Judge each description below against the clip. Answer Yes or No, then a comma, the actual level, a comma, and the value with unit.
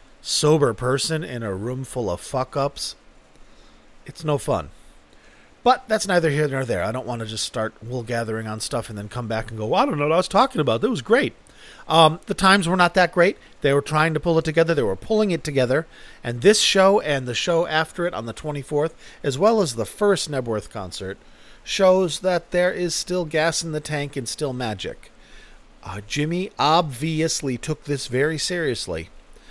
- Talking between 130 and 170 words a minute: No, fast, 205 wpm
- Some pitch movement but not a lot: No, wide, 6.0 semitones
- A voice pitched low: No, medium, 150 Hz